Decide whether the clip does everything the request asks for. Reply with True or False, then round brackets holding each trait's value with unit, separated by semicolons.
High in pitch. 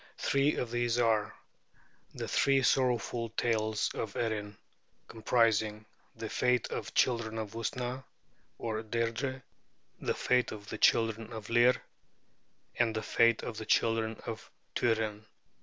False (115 Hz)